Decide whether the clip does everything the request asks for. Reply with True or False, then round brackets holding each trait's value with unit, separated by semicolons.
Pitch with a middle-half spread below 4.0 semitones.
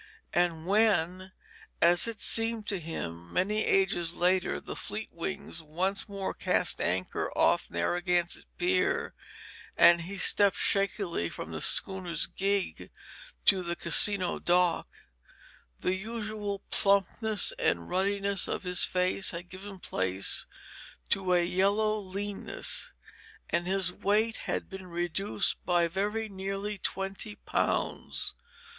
True (2.5 semitones)